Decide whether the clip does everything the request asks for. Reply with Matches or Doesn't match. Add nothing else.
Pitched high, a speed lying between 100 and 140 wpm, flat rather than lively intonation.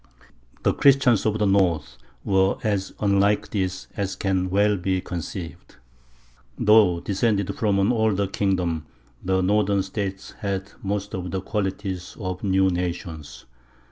Doesn't match